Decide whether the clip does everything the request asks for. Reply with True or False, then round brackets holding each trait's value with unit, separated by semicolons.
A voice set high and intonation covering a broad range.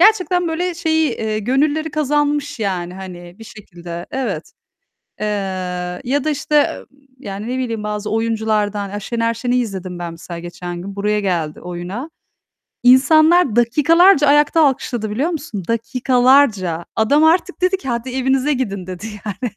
True (235 Hz; 6.6 semitones)